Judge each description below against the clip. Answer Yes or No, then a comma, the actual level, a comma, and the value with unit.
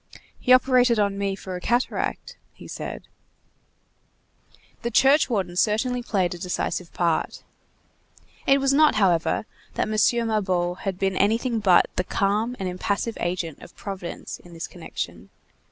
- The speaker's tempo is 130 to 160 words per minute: Yes, average, 145 wpm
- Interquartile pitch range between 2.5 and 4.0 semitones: No, average, 4.7 semitones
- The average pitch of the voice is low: No, high, 200 Hz